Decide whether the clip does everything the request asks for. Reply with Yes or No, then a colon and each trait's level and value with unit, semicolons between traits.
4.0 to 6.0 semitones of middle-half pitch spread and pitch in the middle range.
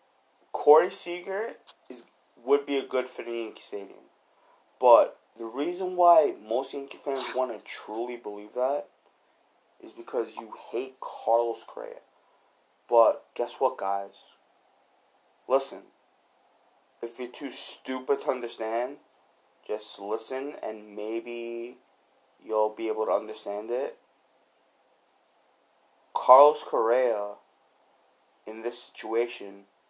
No: average, 4.4 semitones; low, 120 Hz